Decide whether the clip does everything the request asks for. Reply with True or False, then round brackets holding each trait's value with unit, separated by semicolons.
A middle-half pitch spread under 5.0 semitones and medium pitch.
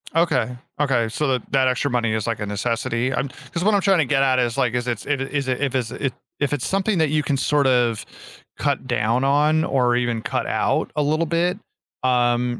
False (3.3 semitones; 130 Hz)